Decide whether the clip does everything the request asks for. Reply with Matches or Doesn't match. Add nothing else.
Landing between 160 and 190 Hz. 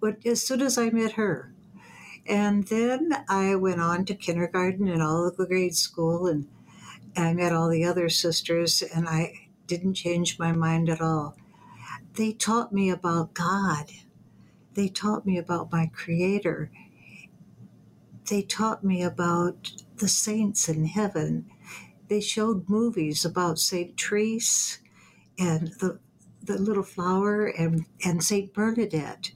Matches